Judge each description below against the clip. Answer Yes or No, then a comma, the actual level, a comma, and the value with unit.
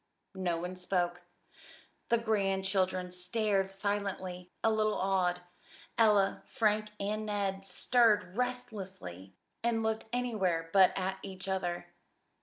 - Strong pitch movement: No, average, 2.9 semitones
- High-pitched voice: Yes, high, 195 Hz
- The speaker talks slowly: Yes, slow, 110 wpm